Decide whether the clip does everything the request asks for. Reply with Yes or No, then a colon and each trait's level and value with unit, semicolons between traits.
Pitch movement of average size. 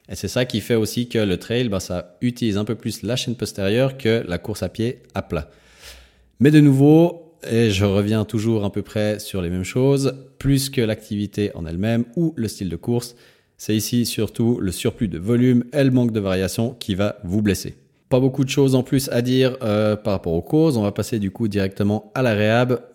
Yes: average, 3.6 semitones